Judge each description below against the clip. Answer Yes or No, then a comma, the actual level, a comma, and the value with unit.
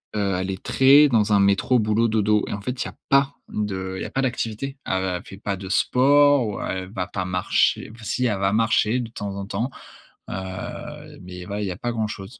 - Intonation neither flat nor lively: Yes, average, 3.6 semitones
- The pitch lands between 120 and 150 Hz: No, low, 105 Hz